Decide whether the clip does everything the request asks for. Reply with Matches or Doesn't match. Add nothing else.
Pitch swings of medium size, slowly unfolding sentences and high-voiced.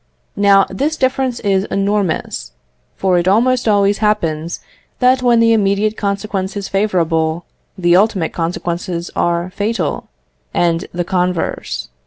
Matches